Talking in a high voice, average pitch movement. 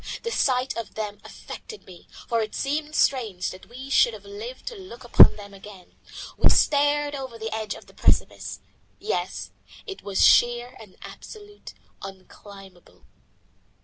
No: high, 235 Hz; wide, 5.7 semitones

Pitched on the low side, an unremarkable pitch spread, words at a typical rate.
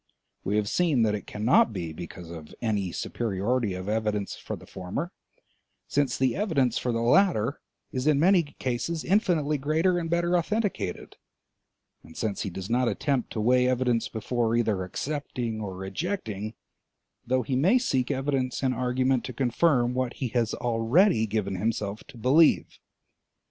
Yes: low, 125 Hz; average, 5.0 semitones; average, 160 wpm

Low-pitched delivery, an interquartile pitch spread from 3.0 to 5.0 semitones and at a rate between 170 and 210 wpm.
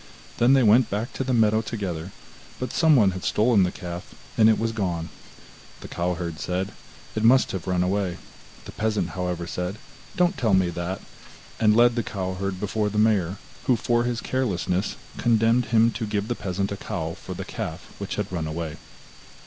Yes: low, 100 Hz; average, 4.1 semitones; average, 190 wpm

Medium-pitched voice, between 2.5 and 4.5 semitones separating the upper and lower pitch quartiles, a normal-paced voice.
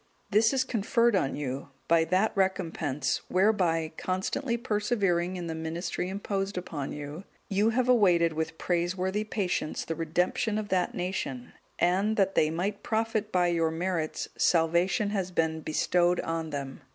Yes: medium, 180 Hz; average, 3.9 semitones; average, 150 wpm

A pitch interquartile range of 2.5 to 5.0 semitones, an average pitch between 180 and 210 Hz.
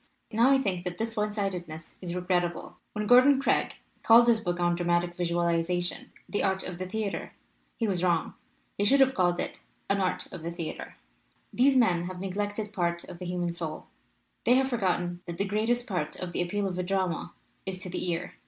Yes: average, 3.3 semitones; medium, 185 Hz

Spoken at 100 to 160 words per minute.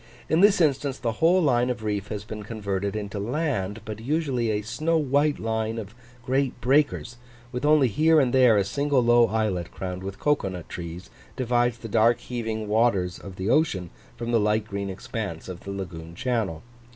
No: average, 190 wpm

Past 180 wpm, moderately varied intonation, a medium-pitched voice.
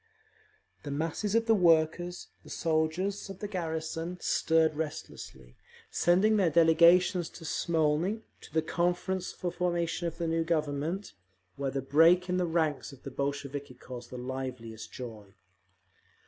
No: average, 145 wpm; average, 3.9 semitones; medium, 165 Hz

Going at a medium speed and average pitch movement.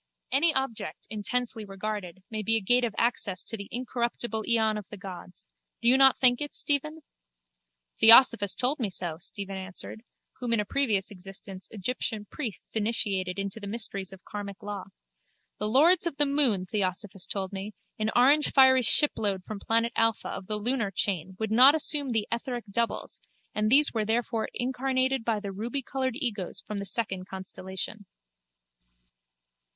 Yes: average, 160 wpm; average, 4.0 semitones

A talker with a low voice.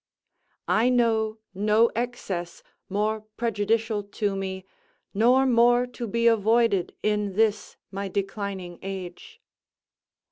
No: high, 215 Hz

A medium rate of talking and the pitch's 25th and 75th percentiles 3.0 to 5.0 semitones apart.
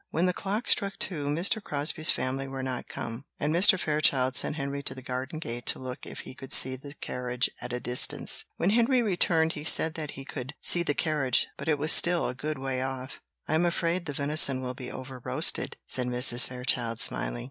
No: fast, 215 wpm; average, 3.9 semitones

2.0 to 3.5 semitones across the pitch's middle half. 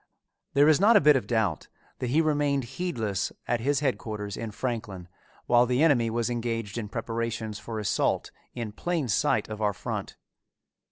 No: average, 4.4 semitones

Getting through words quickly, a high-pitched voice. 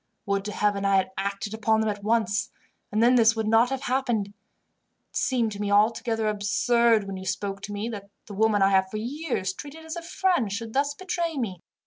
Yes: fast, 215 wpm; high, 220 Hz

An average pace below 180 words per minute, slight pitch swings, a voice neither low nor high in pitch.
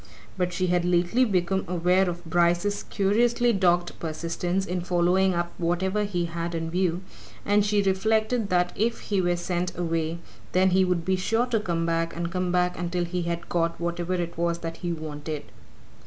No: average, 185 wpm; narrow, 1.9 semitones; medium, 175 Hz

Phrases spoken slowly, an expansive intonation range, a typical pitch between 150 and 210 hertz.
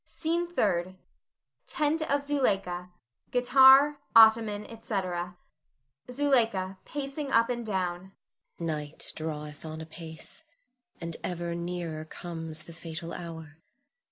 Yes: slow, 100 wpm; wide, 6.9 semitones; medium, 185 Hz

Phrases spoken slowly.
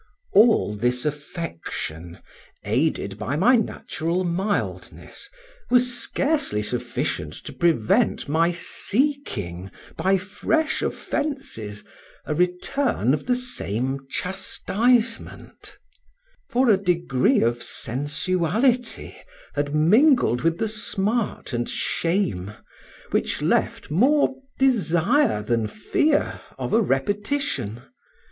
Yes: slow, 95 wpm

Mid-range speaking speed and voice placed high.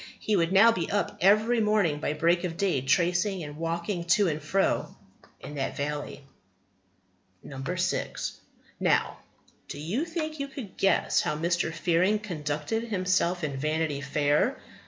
No: average, 145 wpm; medium, 175 Hz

